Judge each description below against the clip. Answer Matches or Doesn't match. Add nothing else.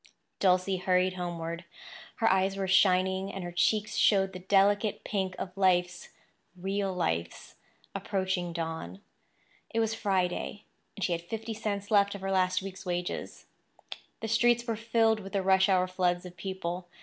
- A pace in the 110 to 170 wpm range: Matches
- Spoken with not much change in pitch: Matches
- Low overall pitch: Doesn't match